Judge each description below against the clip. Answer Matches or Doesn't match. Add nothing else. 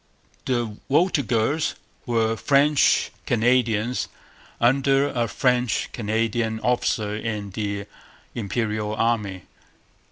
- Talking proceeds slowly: Matches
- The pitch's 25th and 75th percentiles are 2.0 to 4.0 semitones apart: Matches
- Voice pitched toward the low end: Matches